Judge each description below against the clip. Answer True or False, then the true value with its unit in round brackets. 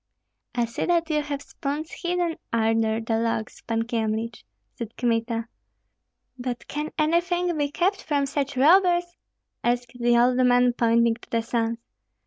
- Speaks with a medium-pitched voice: False (245 Hz)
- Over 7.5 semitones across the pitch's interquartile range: False (4.8 semitones)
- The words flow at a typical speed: True (145 wpm)